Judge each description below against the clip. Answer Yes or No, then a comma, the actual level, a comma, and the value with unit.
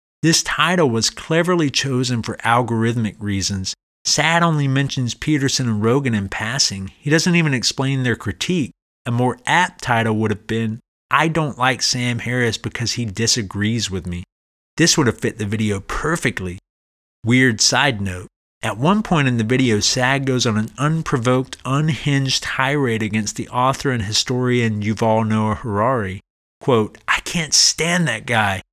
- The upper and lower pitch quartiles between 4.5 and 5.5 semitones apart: No, average, 4.1 semitones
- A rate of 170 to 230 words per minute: No, average, 160 wpm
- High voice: No, low, 120 Hz